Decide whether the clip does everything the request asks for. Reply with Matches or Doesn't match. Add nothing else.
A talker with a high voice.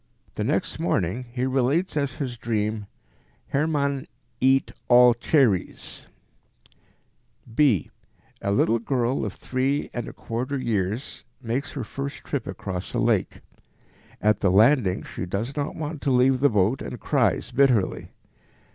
Doesn't match